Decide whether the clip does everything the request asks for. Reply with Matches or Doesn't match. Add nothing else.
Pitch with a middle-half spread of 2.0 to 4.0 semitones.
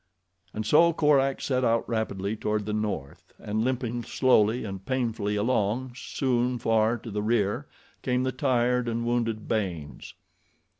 Matches